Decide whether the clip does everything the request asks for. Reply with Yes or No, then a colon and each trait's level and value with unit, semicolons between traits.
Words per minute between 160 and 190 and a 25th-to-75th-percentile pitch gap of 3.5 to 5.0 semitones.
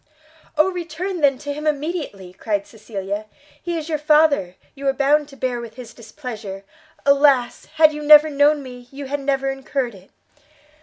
Yes: average, 170 wpm; average, 4.2 semitones